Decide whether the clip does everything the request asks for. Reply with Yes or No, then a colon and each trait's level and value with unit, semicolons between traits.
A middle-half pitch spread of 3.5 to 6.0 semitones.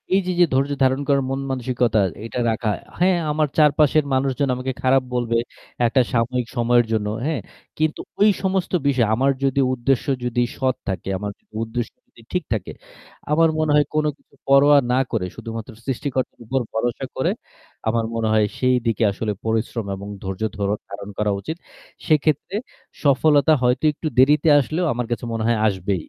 Yes: average, 4.1 semitones